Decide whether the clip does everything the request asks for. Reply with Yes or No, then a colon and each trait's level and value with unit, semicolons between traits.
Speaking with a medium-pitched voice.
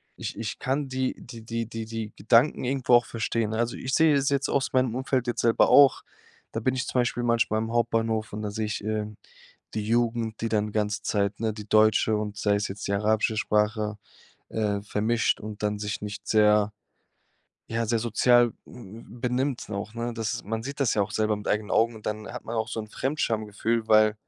No: low, 110 Hz